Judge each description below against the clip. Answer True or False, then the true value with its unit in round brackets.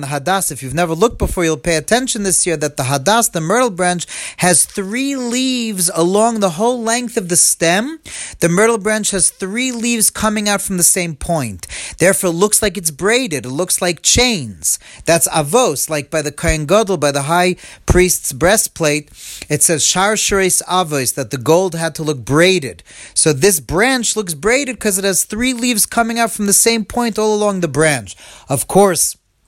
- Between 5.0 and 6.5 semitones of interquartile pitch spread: True (5.4 semitones)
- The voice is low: False (185 Hz)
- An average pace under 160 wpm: False (190 wpm)